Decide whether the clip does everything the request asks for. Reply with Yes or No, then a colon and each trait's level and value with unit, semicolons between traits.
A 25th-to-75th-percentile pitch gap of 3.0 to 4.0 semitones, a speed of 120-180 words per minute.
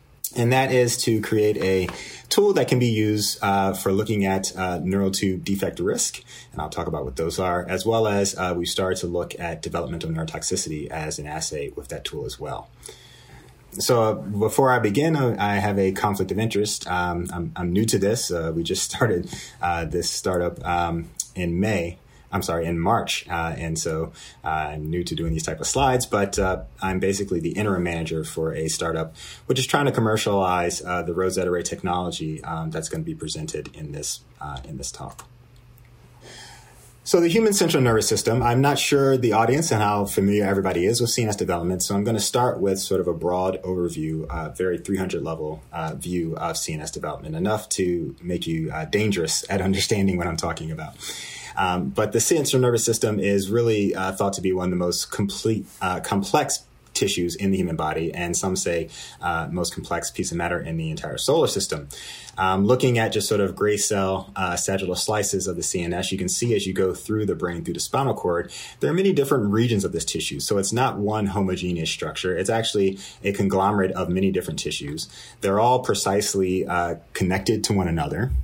No: average, 3.7 semitones; fast, 205 wpm